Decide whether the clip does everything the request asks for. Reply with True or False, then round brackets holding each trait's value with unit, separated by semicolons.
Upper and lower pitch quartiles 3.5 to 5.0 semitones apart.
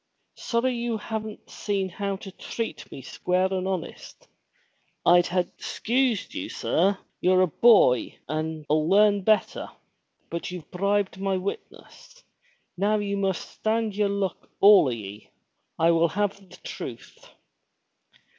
False (3.0 semitones)